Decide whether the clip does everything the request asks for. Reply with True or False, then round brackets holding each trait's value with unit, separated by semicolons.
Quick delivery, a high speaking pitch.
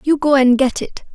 True (260 wpm; 270 Hz)